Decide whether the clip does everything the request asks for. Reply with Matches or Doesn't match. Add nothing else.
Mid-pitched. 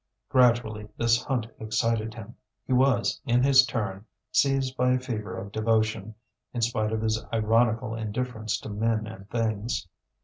Doesn't match